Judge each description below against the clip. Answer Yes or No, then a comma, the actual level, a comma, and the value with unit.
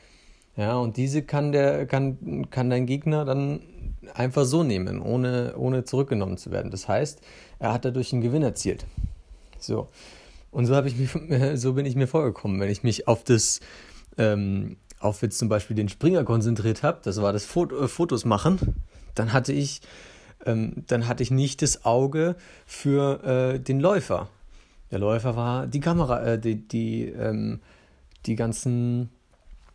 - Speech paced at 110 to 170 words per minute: Yes, average, 165 wpm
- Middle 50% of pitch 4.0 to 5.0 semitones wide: Yes, average, 4.3 semitones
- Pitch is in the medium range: No, low, 120 Hz